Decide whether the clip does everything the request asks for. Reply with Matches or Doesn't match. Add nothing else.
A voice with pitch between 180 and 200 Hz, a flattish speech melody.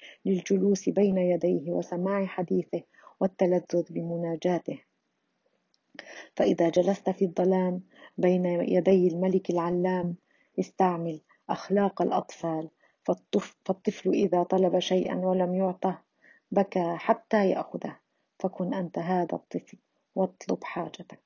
Matches